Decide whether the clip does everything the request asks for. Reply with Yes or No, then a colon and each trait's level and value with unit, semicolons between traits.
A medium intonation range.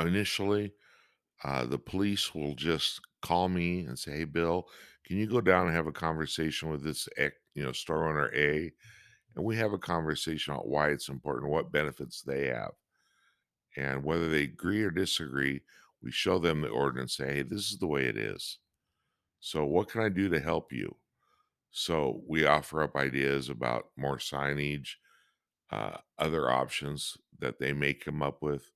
Yes: average, 4.2 semitones